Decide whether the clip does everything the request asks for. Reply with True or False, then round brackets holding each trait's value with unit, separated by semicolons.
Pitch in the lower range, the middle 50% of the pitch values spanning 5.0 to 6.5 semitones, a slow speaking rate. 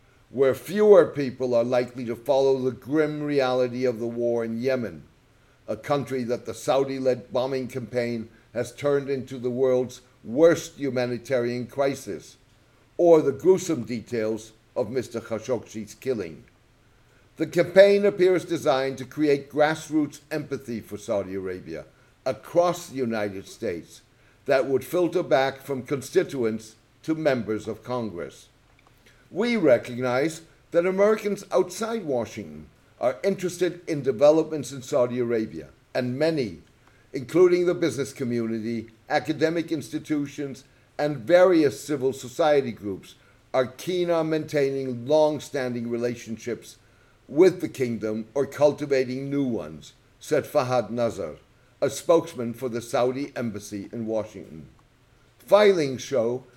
False (130 Hz; 4.2 semitones; 125 wpm)